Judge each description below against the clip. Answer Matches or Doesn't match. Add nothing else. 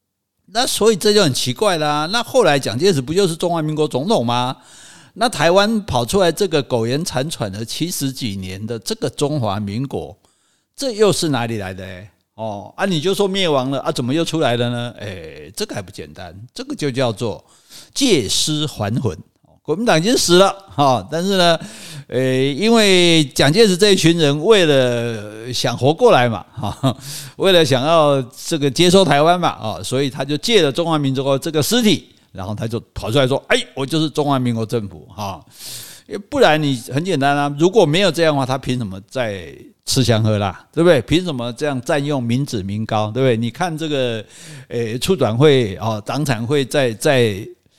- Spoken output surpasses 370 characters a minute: Doesn't match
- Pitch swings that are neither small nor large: Doesn't match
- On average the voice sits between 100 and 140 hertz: Matches